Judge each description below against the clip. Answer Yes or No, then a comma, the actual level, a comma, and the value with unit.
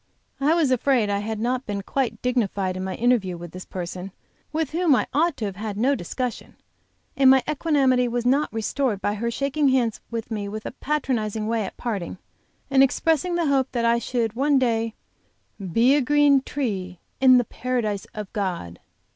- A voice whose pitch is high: Yes, high, 240 Hz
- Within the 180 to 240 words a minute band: Yes, average, 185 wpm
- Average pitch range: Yes, average, 4.6 semitones